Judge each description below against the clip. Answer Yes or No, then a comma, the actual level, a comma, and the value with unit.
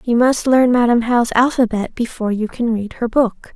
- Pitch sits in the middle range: No, high, 235 Hz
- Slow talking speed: No, fast, 205 wpm